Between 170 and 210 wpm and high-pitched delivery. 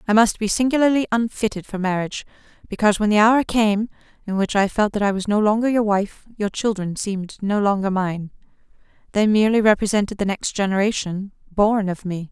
Yes: average, 180 wpm; high, 205 Hz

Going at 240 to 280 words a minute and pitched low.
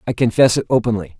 No: average, 200 wpm; low, 120 Hz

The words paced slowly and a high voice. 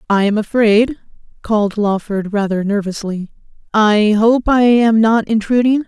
Yes: slow, 120 wpm; high, 215 Hz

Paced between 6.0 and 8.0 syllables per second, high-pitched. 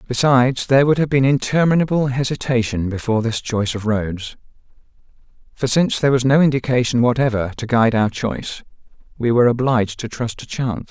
No: 6.2 syllables/s; low, 125 Hz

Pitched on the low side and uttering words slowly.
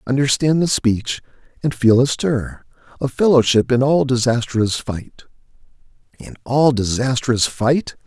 Yes: low, 125 Hz; slow, 125 wpm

